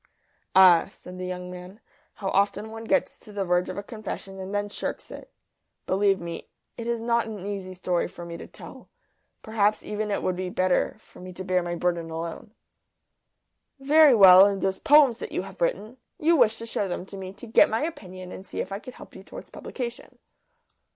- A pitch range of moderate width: Yes, average, 3.4 semitones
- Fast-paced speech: Yes, fast, 210 wpm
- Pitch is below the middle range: No, high, 195 Hz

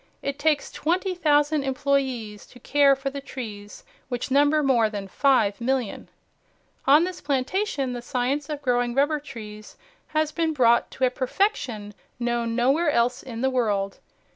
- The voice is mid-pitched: No, very high, 265 Hz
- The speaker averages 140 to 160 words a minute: Yes, average, 150 wpm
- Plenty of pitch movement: No, average, 3.6 semitones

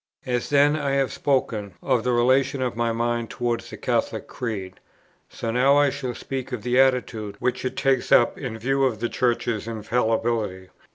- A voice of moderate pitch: No, low, 120 Hz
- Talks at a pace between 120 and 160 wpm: No, average, 190 wpm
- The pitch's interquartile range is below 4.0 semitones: Yes, narrow, 2.6 semitones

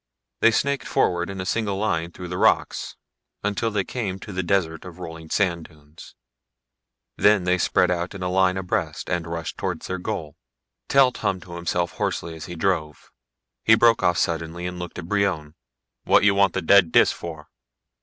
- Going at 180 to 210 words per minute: Yes, average, 185 wpm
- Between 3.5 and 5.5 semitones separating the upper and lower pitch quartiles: No, average, 2.8 semitones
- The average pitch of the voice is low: Yes, very low, 90 Hz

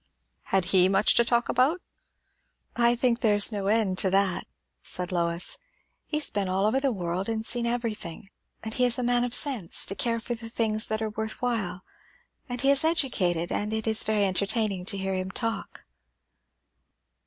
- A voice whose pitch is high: Yes, high, 220 Hz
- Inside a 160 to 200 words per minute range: Yes, average, 190 wpm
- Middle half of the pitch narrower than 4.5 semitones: Yes, average, 3.7 semitones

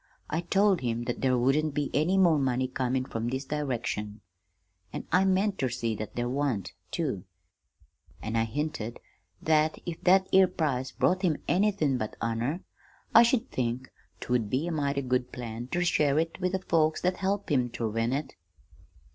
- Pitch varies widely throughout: Yes, wide, 5.9 semitones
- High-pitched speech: No, medium, 140 Hz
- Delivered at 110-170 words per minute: No, average, 180 wpm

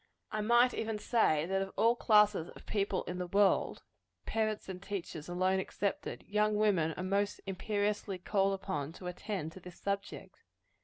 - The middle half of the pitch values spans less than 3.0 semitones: Yes, narrow, 2.5 semitones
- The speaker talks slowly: No, average, 165 wpm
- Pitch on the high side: Yes, high, 195 Hz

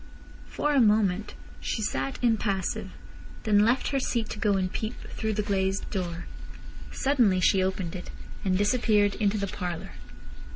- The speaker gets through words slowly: No, average, 155 wpm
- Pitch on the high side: Yes, high, 205 Hz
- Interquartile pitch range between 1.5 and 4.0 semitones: Yes, average, 2.7 semitones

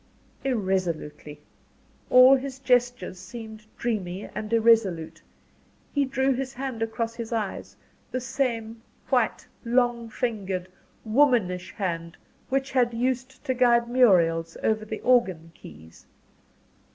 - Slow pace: Yes, slow, 115 wpm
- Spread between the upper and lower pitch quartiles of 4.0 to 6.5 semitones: Yes, average, 5.1 semitones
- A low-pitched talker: No, high, 230 Hz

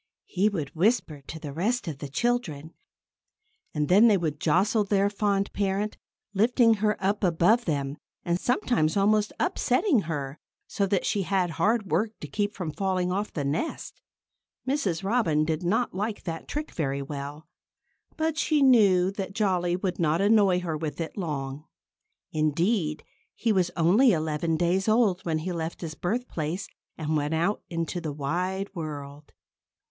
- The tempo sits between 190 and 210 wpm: No, average, 160 wpm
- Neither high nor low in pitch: Yes, medium, 180 Hz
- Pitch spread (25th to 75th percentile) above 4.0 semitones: Yes, average, 4.8 semitones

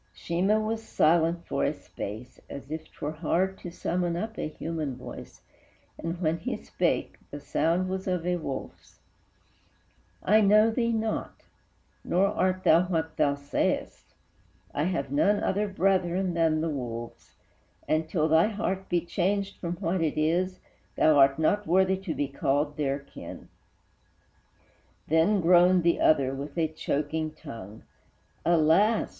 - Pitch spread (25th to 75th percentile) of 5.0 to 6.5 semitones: No, average, 3.6 semitones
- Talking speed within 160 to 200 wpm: No, average, 150 wpm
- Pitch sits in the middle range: Yes, medium, 170 Hz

